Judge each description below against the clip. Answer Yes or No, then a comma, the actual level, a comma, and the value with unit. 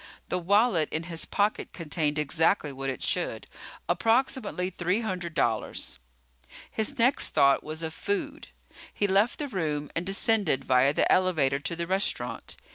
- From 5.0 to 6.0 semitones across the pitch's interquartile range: Yes, wide, 5.5 semitones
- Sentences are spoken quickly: No, average, 150 wpm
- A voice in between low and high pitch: Yes, medium, 175 Hz